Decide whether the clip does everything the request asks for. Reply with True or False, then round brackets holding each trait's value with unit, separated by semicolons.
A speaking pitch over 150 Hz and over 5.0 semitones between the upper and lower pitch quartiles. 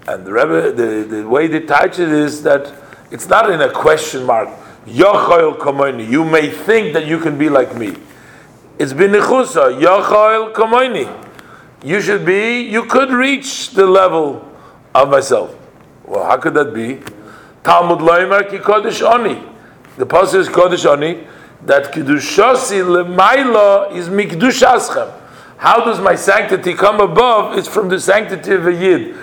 True (190 Hz; 5.6 semitones)